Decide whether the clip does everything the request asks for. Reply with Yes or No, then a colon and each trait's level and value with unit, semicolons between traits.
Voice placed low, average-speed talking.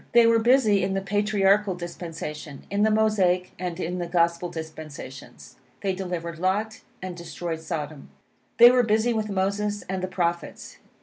No: medium, 185 Hz; average, 160 wpm